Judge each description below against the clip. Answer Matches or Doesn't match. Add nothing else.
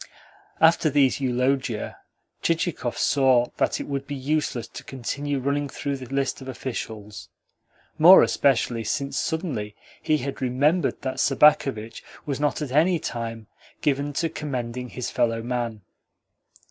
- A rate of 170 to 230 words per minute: Doesn't match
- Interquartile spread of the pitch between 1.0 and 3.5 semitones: Matches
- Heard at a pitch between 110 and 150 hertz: Matches